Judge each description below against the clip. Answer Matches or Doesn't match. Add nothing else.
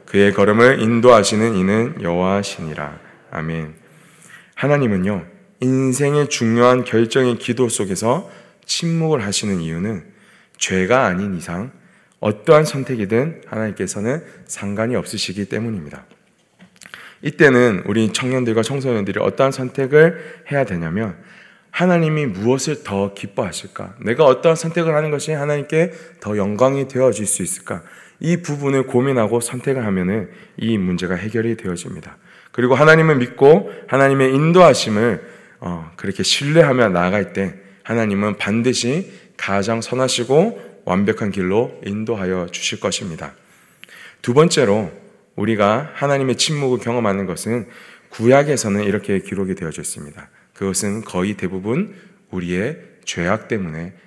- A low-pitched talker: Matches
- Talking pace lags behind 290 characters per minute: Doesn't match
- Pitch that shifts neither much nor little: Doesn't match